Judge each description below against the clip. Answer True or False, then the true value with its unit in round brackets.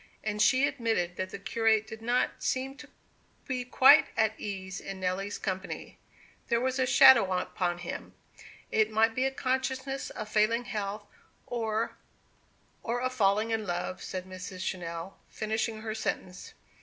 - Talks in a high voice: True (220 Hz)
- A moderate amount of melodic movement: True (4.3 semitones)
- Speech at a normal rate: True (150 wpm)